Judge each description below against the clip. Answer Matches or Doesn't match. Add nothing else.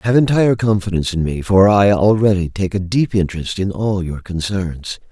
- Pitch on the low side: Matches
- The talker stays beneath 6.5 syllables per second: Matches